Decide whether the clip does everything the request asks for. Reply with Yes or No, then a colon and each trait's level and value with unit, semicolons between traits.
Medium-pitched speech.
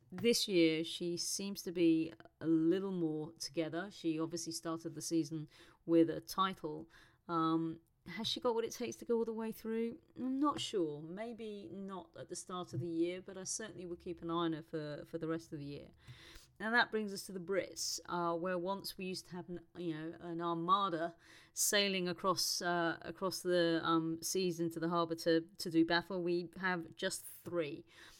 Yes: medium, 170 Hz